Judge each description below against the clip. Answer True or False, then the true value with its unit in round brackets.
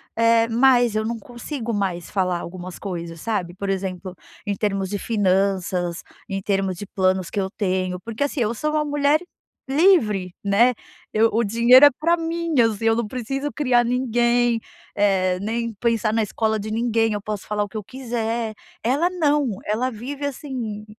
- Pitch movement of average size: True (3.9 semitones)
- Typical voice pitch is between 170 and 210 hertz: False (225 Hz)